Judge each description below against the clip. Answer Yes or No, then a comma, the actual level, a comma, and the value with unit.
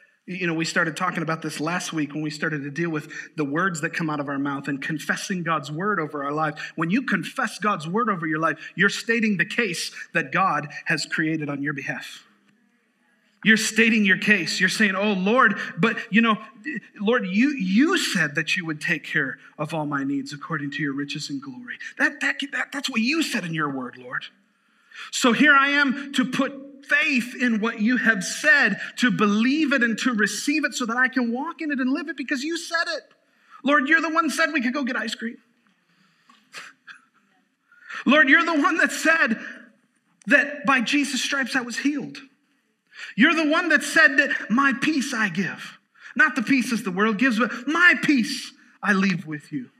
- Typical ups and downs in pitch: No, wide, 7.5 semitones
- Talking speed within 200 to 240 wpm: Yes, fast, 205 wpm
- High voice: Yes, high, 230 Hz